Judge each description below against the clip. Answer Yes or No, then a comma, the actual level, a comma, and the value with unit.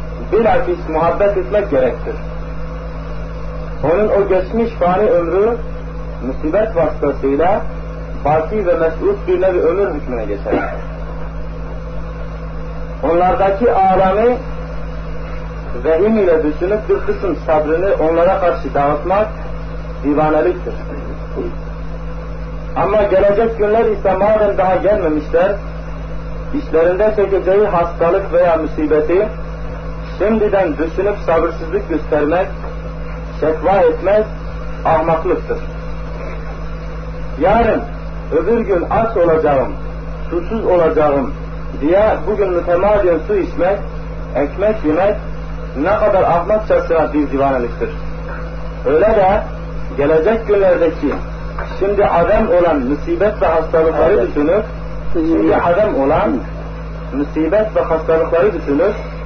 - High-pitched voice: No, medium, 165 Hz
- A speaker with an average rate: No, slow, 90 wpm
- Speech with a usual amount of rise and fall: Yes, average, 3.4 semitones